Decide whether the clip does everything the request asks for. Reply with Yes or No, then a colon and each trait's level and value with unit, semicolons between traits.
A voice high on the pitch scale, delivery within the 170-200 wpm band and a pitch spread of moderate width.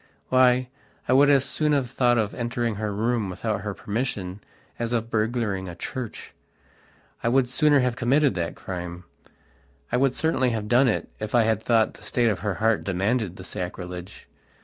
No: low, 115 Hz; average, 180 wpm; average, 3.9 semitones